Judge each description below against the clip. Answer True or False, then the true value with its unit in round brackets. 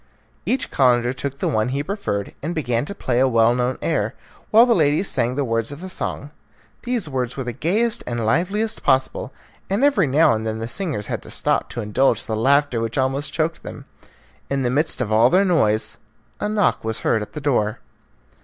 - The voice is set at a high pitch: False (135 Hz)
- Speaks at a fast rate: True (210 wpm)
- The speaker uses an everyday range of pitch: False (6.2 semitones)